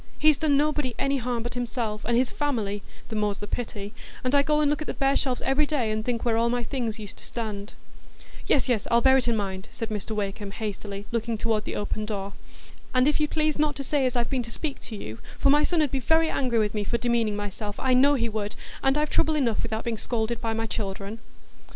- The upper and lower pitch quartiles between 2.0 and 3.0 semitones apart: No, average, 4.2 semitones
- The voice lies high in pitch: Yes, high, 235 Hz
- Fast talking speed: Yes, fast, 245 wpm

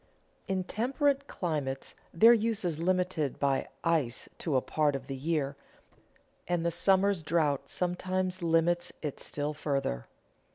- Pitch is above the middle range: No, medium, 165 Hz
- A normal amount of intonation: Yes, average, 4.4 semitones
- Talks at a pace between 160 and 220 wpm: No, slow, 135 wpm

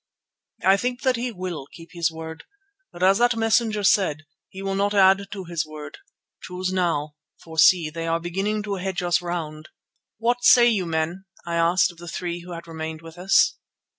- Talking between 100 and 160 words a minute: No, average, 195 wpm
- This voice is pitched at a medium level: Yes, medium, 180 Hz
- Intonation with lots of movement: No, average, 3.2 semitones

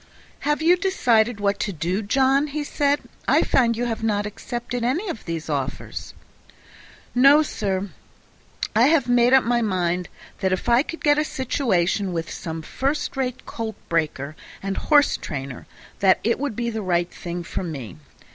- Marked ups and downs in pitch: Yes, wide, 6.9 semitones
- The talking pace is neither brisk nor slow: Yes, average, 165 wpm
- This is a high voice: Yes, high, 225 Hz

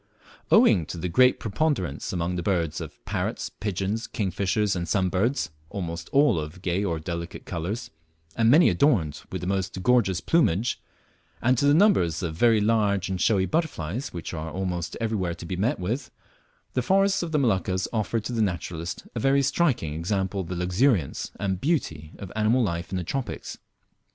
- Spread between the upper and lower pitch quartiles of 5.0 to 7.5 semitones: Yes, wide, 5.5 semitones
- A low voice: Yes, very low, 95 Hz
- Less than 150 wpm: No, average, 175 wpm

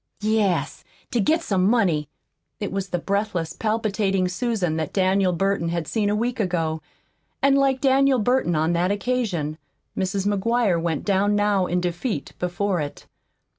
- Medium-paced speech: Yes, average, 155 wpm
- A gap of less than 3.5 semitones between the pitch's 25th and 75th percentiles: No, average, 3.9 semitones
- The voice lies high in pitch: Yes, high, 195 Hz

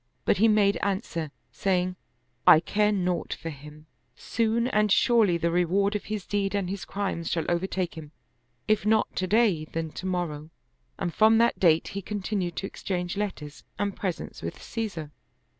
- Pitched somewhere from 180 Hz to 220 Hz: Yes, high, 190 Hz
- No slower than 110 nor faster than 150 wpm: No, average, 175 wpm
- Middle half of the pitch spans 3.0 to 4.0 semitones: Yes, average, 3.7 semitones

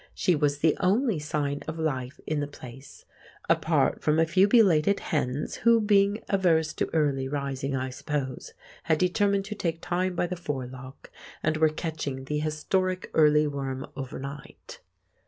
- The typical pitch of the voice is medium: Yes, medium, 155 Hz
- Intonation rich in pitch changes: No, average, 4.6 semitones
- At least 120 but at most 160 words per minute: Yes, average, 155 wpm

